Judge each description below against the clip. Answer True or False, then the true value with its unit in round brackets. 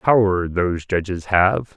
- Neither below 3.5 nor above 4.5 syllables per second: True (4.1 syllables/s)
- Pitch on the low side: True (95 Hz)